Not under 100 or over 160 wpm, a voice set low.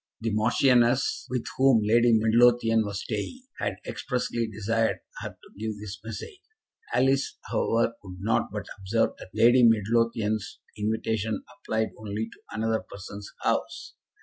Yes: slow, 135 wpm; low, 110 Hz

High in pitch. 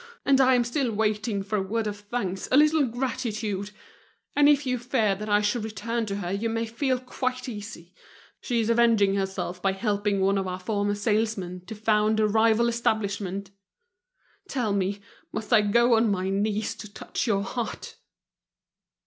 Yes: high, 215 Hz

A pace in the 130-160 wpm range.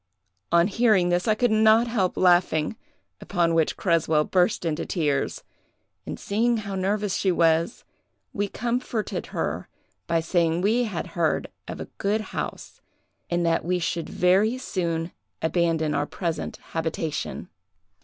Yes: average, 140 wpm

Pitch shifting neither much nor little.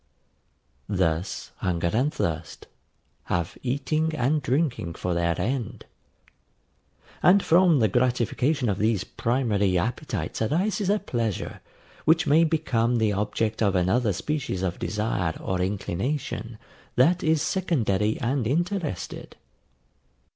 No: wide, 7.5 semitones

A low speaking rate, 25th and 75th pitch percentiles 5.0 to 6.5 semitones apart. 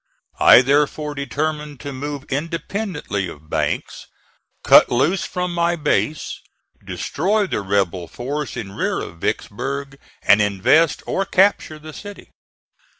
Yes: slow, 125 wpm; wide, 5.5 semitones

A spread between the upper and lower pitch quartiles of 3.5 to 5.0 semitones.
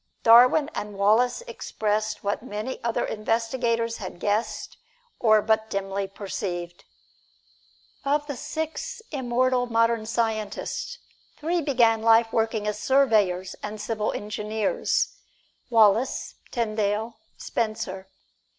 No: average, 2.8 semitones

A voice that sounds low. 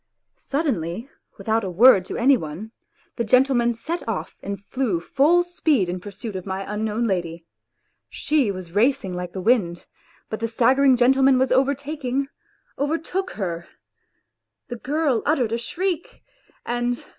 No: high, 235 Hz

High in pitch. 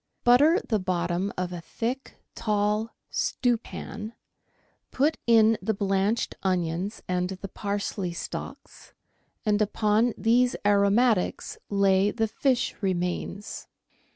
Yes: high, 205 Hz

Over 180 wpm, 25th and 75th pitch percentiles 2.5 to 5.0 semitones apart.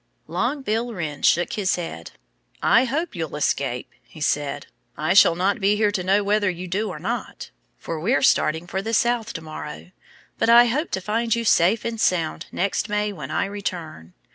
No: average, 190 wpm; wide, 5.4 semitones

